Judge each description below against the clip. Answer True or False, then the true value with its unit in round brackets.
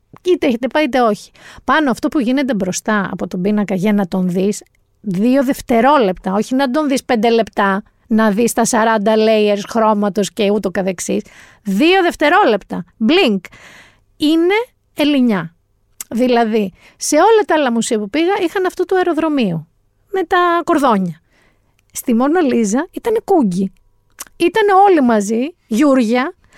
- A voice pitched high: True (235 Hz)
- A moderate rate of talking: True (145 wpm)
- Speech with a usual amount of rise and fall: False (6.9 semitones)